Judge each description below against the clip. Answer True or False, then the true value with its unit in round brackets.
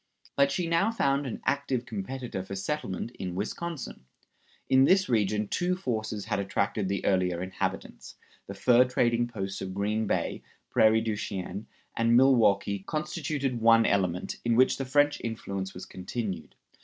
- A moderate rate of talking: True (155 wpm)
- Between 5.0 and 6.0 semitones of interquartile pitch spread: True (5.3 semitones)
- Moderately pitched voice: False (110 Hz)